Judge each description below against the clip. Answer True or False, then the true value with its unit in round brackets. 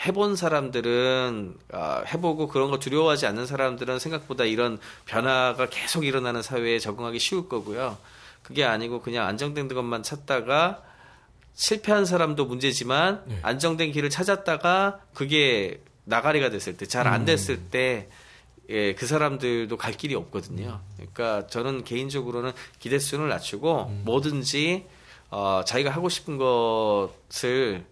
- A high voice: False (130 Hz)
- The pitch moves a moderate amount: True (4.6 semitones)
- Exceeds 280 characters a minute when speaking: True (310 characters per minute)